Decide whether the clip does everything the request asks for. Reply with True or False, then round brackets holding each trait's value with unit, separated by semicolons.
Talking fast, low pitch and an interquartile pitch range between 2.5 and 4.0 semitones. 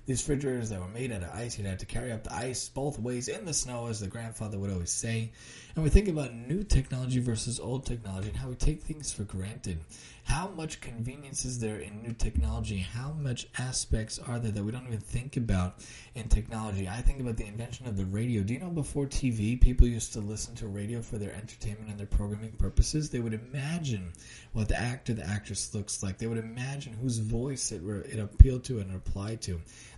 True (225 wpm; 115 Hz; 3.3 semitones)